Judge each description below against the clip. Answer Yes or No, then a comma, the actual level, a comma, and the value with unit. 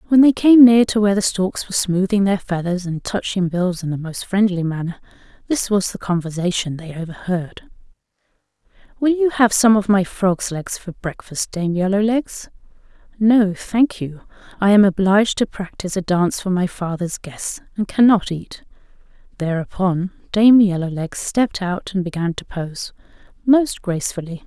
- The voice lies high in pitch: Yes, high, 195 Hz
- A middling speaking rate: Yes, average, 160 wpm